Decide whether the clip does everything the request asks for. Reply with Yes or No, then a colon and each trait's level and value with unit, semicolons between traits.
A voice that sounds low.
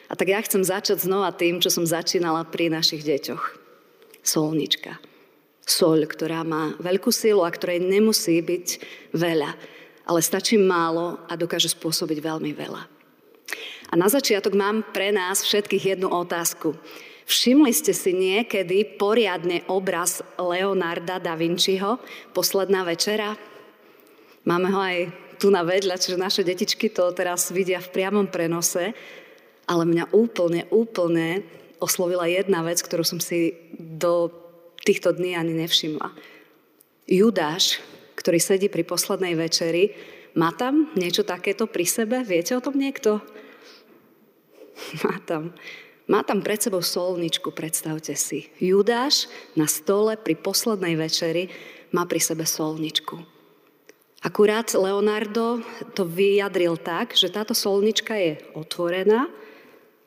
No: medium, 185 Hz